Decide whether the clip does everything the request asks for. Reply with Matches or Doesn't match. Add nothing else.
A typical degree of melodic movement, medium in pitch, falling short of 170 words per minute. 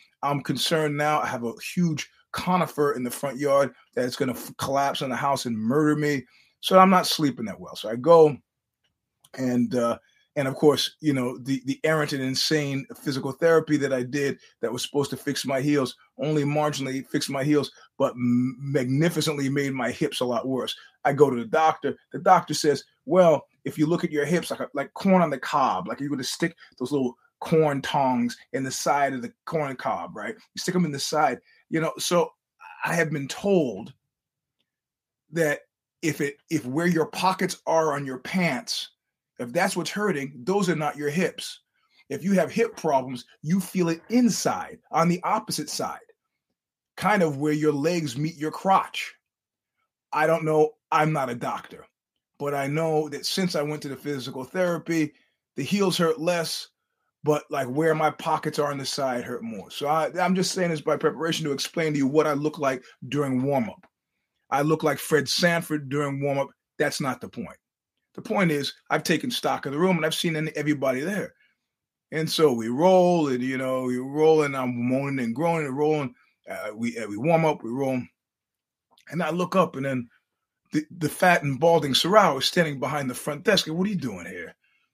Doesn't match